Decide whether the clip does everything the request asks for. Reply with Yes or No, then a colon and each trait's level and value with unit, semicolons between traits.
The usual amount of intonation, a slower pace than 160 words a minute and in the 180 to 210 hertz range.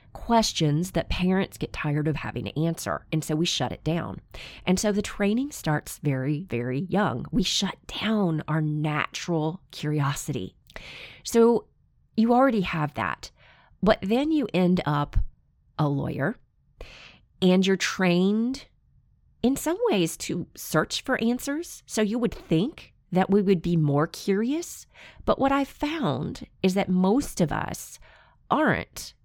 No: wide, 6.6 semitones; average, 145 wpm; medium, 185 Hz